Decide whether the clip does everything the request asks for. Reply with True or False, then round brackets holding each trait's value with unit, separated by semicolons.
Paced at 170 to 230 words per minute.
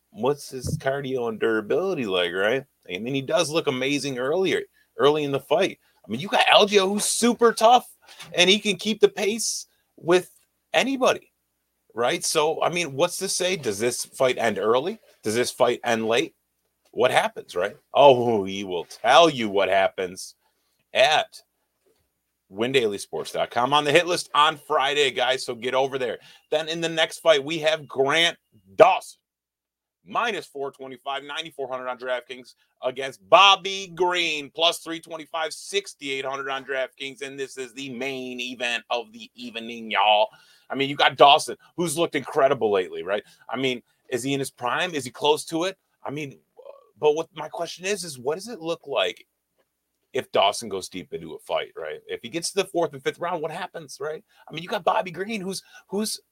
True (180 wpm)